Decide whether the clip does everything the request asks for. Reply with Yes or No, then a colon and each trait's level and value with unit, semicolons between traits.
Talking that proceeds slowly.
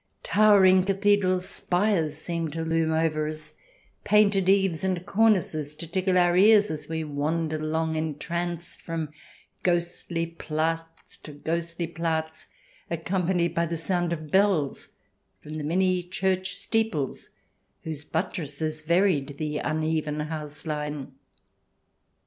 Yes: slow, 125 wpm